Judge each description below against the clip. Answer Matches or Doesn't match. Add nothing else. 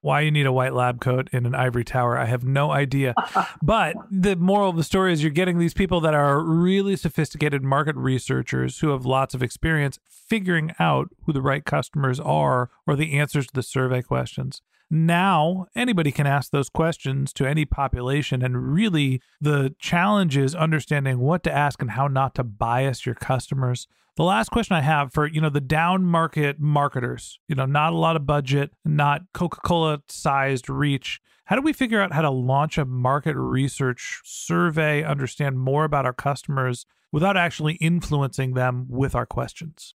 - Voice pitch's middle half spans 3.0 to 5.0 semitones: Matches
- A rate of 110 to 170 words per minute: Doesn't match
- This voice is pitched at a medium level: Matches